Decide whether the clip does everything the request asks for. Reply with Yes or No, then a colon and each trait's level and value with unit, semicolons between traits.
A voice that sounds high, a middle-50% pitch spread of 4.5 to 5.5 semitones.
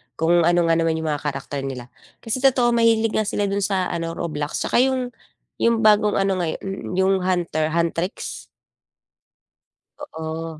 No: medium, 180 Hz; average, 5.1 semitones